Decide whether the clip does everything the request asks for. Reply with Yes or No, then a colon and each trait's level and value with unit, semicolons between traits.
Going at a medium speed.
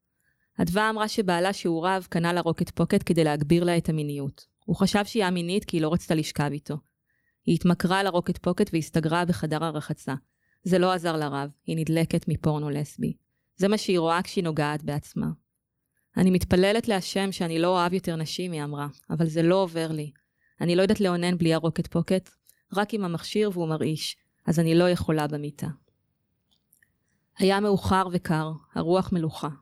No: fast, 170 wpm